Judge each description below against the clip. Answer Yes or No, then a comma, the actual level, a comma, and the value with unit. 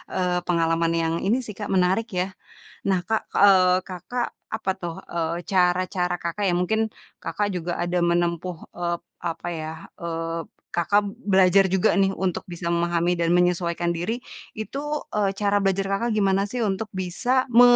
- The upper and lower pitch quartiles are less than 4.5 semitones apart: Yes, narrow, 2.6 semitones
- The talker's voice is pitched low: No, medium, 180 Hz